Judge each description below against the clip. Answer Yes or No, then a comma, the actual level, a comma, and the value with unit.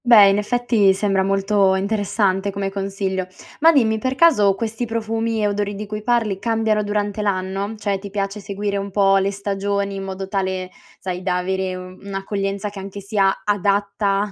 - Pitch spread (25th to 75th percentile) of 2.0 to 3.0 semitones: No, narrow, 1.5 semitones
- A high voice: Yes, high, 200 Hz